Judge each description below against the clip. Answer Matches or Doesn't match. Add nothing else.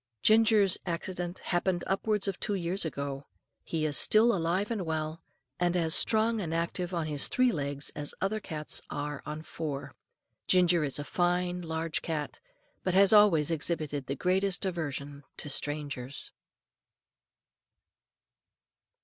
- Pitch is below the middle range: Doesn't match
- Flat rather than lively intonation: Doesn't match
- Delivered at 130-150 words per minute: Matches